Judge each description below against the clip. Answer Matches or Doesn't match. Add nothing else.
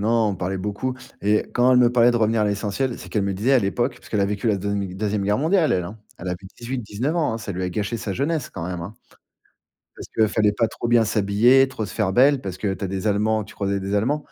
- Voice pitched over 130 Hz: Doesn't match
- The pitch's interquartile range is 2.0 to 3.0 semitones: Doesn't match